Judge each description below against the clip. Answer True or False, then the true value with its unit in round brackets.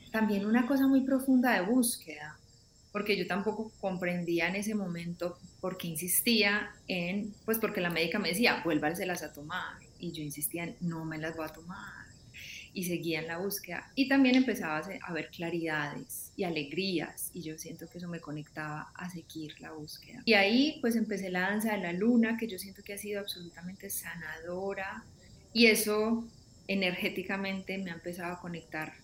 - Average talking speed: True (180 wpm)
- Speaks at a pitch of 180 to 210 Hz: True (185 Hz)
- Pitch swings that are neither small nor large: True (4.0 semitones)